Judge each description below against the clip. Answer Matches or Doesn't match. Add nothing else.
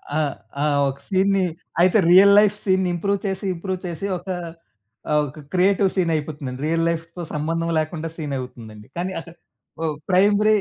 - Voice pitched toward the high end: Doesn't match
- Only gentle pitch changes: Doesn't match